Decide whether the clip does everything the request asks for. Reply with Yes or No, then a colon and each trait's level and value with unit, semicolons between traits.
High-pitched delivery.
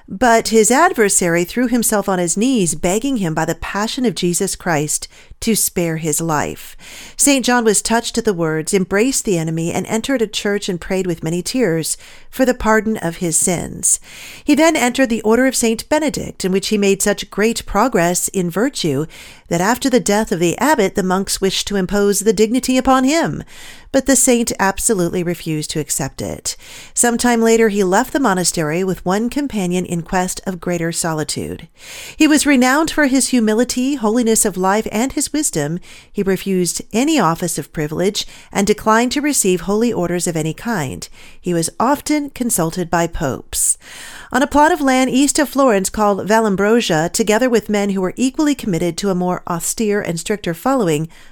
Yes: high, 210 Hz